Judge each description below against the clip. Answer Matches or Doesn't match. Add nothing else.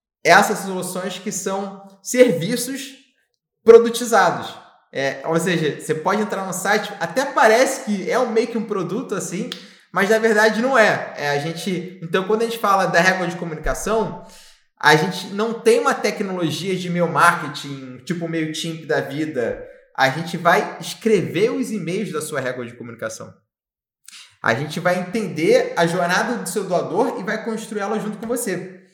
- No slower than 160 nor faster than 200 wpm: Matches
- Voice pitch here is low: Doesn't match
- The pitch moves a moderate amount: Matches